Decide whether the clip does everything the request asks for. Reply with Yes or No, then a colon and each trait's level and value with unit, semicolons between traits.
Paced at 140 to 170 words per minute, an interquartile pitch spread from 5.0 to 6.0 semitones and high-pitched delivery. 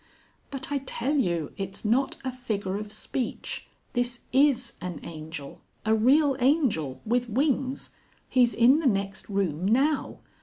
Yes: average, 145 wpm; wide, 5.4 semitones; high, 235 Hz